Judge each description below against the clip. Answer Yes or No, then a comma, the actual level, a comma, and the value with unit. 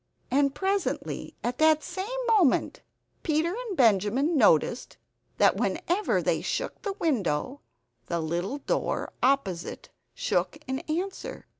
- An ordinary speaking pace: No, slow, 120 wpm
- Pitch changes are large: Yes, wide, 8.6 semitones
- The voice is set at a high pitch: Yes, very high, 290 Hz